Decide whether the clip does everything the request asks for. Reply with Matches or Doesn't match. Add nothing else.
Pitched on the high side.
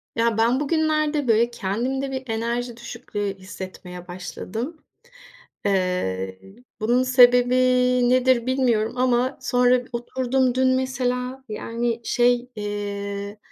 Matches